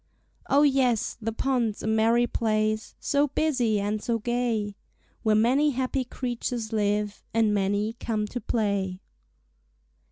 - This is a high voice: Yes, high, 225 Hz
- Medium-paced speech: No, slow, 130 wpm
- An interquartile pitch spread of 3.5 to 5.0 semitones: No, average, 2.7 semitones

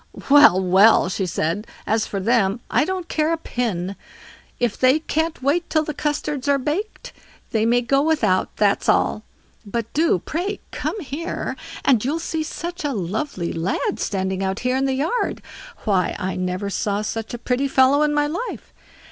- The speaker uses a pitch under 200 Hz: No, very high, 255 Hz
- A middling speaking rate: Yes, average, 175 wpm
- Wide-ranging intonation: Yes, wide, 7.2 semitones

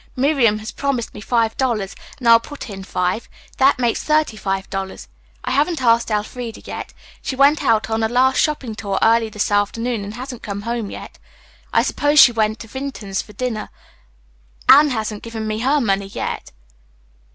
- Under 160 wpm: No, average, 185 wpm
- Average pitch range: Yes, average, 3.6 semitones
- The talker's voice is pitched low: No, high, 230 Hz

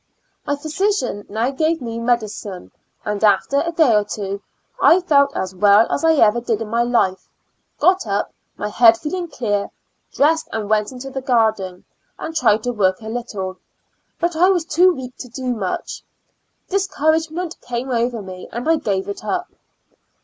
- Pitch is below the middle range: No, high, 240 Hz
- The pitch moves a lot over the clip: Yes, wide, 6.9 semitones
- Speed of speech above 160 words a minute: Yes, average, 170 wpm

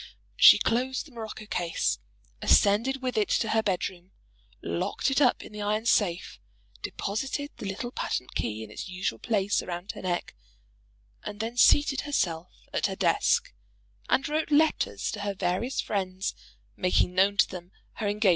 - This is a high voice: Yes, high, 205 Hz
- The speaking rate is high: No, average, 165 wpm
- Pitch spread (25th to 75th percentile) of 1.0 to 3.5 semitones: No, average, 5.0 semitones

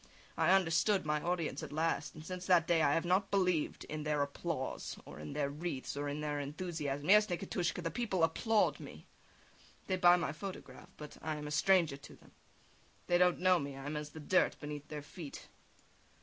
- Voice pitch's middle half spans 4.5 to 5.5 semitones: No, average, 3.6 semitones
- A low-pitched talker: No, medium, 160 Hz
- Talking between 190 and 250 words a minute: Yes, average, 200 wpm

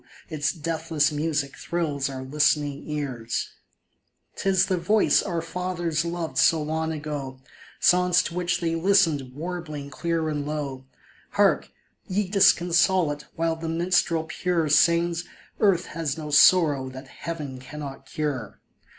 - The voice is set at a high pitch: No, medium, 160 Hz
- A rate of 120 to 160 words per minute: Yes, average, 140 wpm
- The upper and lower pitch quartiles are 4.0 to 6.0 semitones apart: No, average, 3.0 semitones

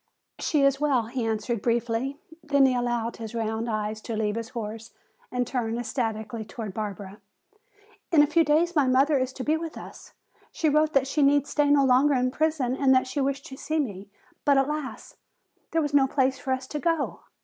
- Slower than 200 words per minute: No, fast, 205 wpm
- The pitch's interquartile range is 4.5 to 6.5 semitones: No, average, 4.1 semitones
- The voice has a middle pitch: No, very high, 260 Hz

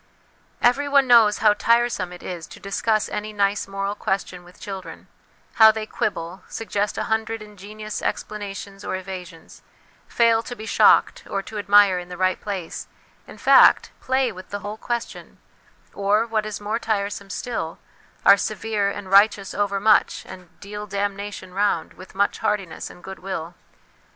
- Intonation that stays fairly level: Yes, narrow, 2.1 semitones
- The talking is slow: No, average, 160 wpm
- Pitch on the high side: Yes, high, 205 Hz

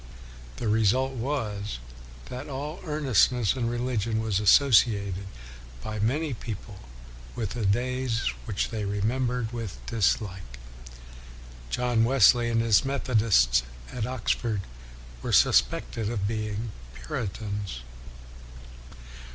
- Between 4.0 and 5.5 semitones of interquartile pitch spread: No, average, 3.5 semitones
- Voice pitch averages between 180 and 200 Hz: No, low, 115 Hz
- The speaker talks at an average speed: No, slow, 105 wpm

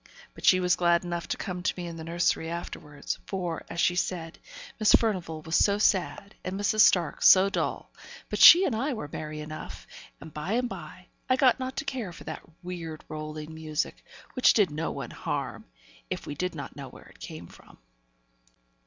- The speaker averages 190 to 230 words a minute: Yes, average, 195 wpm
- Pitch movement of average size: Yes, average, 4.2 semitones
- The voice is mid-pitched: Yes, medium, 175 Hz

